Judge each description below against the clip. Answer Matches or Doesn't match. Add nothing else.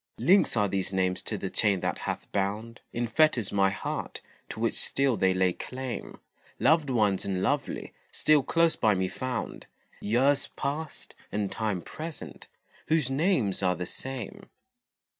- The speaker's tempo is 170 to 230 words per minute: Doesn't match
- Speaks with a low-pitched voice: Matches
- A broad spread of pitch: Matches